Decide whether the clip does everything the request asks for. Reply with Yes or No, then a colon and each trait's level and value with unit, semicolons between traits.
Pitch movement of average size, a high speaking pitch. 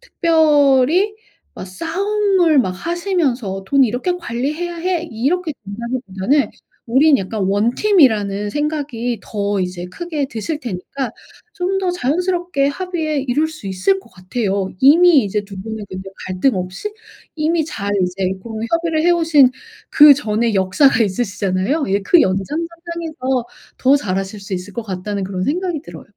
No: wide, 8.6 semitones; very high, 260 Hz